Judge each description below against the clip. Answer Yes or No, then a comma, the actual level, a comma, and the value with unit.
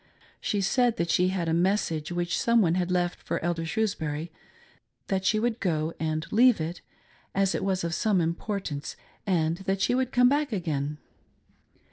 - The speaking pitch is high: No, medium, 180 Hz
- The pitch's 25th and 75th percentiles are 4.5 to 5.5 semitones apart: No, average, 4.1 semitones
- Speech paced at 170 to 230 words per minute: Yes, average, 175 wpm